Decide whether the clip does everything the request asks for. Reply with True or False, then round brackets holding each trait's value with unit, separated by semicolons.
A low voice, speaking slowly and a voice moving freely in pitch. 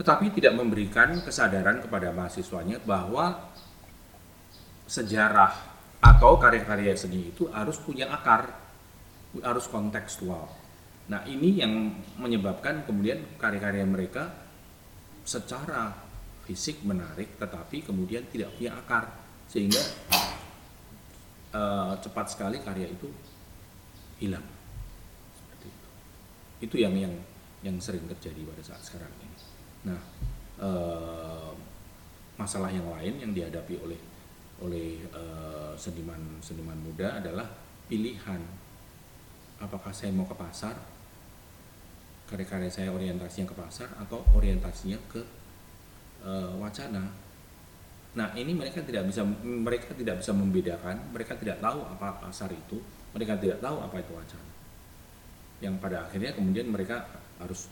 False (95 Hz; 110 wpm; 3.0 semitones)